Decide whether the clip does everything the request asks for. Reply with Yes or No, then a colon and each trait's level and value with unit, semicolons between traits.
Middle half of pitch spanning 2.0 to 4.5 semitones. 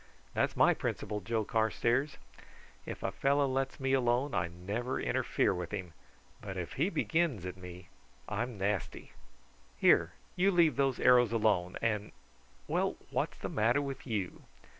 No: wide, 5.6 semitones